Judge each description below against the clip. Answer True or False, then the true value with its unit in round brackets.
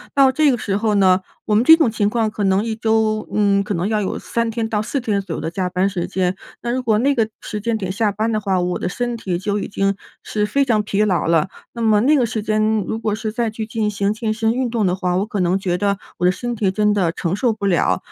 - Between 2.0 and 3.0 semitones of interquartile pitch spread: True (2.6 semitones)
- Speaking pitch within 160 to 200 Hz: False (210 Hz)